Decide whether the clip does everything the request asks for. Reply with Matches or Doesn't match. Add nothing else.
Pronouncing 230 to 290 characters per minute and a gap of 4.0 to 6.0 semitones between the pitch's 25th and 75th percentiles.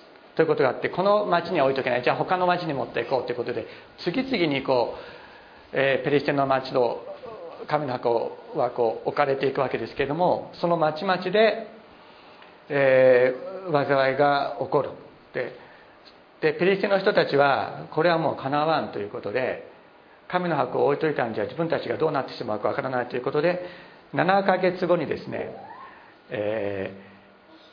Doesn't match